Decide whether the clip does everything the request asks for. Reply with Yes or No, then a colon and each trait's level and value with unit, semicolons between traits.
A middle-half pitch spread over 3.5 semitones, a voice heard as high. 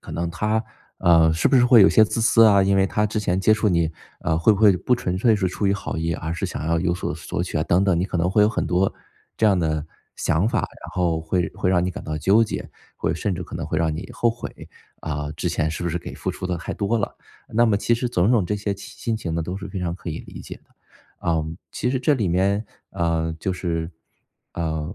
No: average, 4.1 semitones; very low, 90 Hz